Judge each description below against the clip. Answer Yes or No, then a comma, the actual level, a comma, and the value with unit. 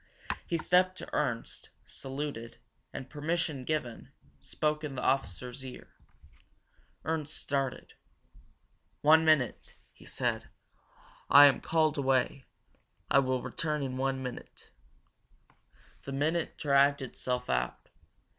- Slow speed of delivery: Yes, slow, 115 wpm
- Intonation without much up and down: No, average, 3.0 semitones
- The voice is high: No, medium, 140 Hz